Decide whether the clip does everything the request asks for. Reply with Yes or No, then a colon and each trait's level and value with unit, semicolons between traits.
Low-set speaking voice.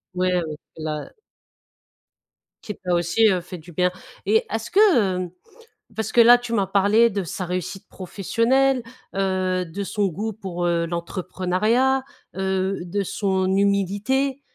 No: high, 195 Hz